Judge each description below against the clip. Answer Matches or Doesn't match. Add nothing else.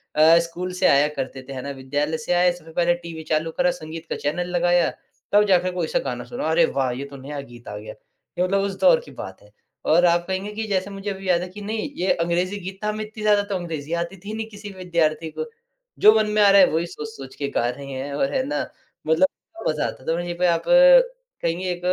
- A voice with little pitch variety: Doesn't match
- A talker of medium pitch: Matches